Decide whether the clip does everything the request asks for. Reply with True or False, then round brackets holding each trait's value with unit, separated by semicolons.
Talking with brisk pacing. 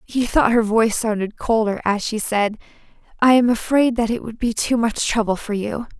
True (210 wpm)